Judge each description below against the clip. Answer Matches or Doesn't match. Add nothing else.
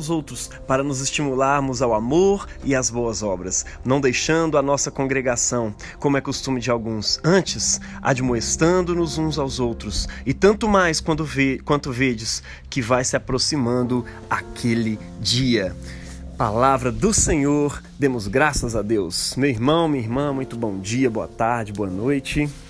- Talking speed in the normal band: Matches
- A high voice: Doesn't match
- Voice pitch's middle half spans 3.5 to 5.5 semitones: Matches